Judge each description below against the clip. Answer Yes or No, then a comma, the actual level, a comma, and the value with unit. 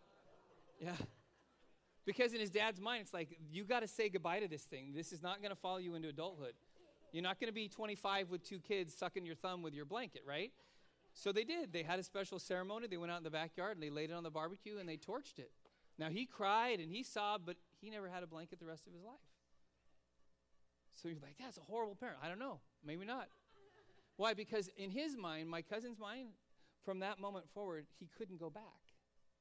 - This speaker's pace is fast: Yes, fast, 225 wpm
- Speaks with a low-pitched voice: No, medium, 185 Hz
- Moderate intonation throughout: Yes, average, 4.8 semitones